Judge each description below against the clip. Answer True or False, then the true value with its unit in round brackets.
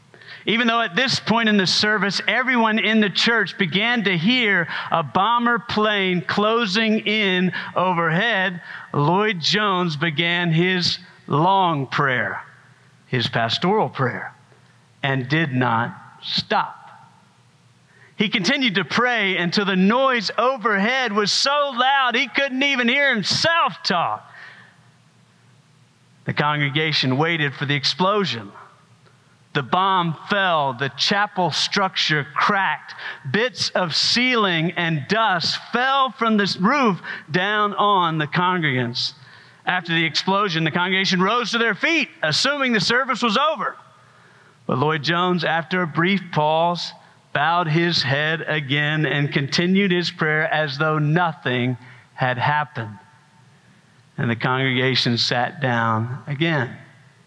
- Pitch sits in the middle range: True (180 Hz)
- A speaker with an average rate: False (125 wpm)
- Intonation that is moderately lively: False (6.2 semitones)